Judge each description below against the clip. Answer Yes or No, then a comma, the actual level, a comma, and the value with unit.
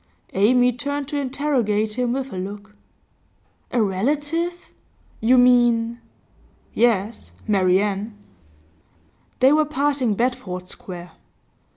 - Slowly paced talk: Yes, slow, 100 wpm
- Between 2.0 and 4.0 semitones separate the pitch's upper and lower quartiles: No, average, 4.7 semitones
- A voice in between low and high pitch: No, high, 240 Hz